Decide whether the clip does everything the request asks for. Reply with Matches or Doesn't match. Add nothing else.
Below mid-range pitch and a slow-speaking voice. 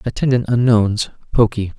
Matches